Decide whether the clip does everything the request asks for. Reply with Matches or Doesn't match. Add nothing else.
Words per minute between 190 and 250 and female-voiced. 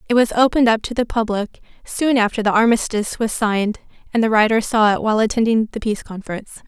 Matches